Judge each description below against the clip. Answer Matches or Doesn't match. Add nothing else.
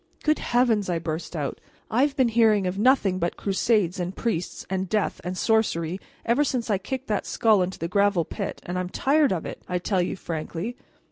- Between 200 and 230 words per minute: Matches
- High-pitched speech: Matches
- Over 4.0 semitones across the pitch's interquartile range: Matches